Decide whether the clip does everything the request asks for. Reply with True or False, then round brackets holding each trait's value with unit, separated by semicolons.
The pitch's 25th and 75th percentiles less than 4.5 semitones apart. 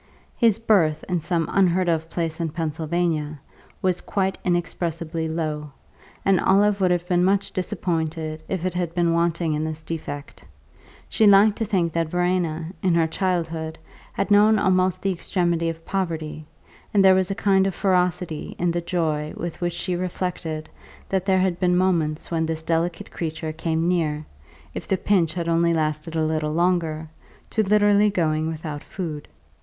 True (2.6 semitones)